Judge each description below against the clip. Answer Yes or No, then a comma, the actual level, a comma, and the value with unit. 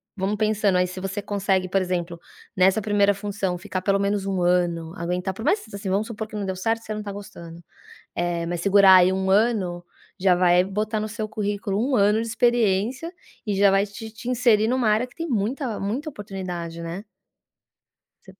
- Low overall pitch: No, high, 200 Hz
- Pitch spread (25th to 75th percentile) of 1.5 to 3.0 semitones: Yes, average, 2.7 semitones